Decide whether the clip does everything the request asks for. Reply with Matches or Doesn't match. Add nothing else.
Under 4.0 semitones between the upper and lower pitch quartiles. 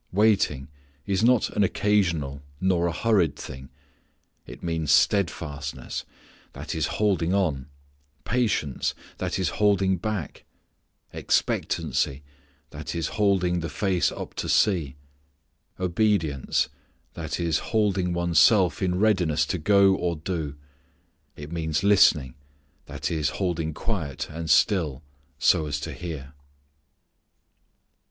Doesn't match